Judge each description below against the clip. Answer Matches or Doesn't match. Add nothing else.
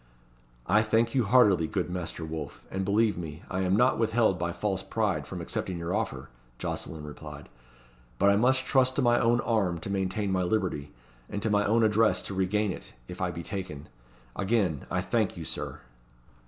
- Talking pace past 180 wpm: Matches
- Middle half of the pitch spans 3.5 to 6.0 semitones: Matches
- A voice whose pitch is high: Doesn't match